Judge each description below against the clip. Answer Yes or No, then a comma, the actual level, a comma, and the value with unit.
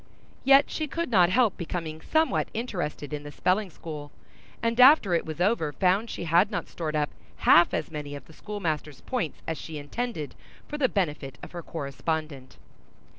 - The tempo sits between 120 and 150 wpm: No, average, 180 wpm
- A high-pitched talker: No, medium, 170 Hz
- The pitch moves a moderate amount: No, wide, 6.3 semitones